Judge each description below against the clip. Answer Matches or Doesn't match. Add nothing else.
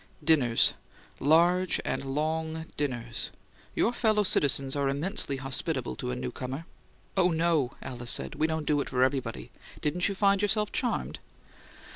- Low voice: Doesn't match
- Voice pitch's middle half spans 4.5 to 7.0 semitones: Matches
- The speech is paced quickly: Doesn't match